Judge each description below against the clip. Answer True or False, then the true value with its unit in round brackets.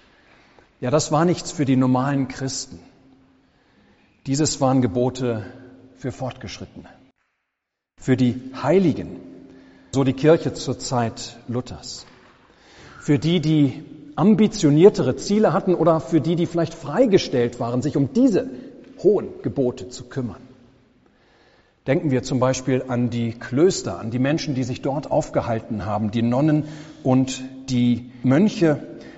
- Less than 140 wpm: True (125 wpm)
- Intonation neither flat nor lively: True (3.5 semitones)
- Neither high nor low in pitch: False (130 Hz)